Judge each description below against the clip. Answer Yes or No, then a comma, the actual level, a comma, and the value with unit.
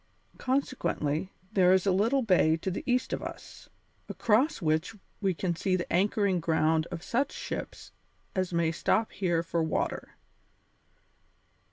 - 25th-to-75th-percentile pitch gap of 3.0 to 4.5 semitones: Yes, average, 4.1 semitones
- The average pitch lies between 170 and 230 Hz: Yes, medium, 185 Hz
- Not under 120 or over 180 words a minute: Yes, average, 145 wpm